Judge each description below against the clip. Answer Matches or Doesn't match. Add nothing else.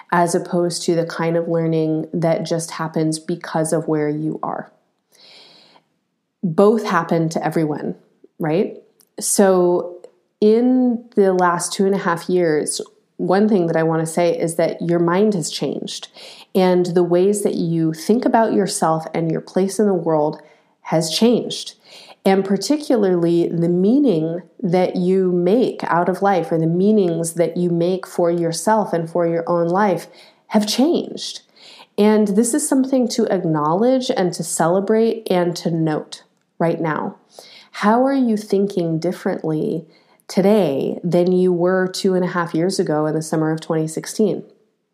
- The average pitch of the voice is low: Doesn't match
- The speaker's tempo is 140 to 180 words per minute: Matches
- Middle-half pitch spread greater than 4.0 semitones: Doesn't match